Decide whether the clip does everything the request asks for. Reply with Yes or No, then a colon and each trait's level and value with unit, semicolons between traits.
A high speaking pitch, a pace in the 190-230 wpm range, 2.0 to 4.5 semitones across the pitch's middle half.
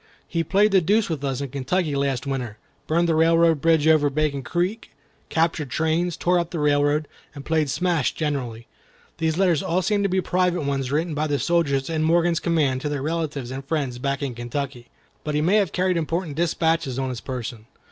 No: medium, 155 Hz; average, 200 wpm; average, 3.5 semitones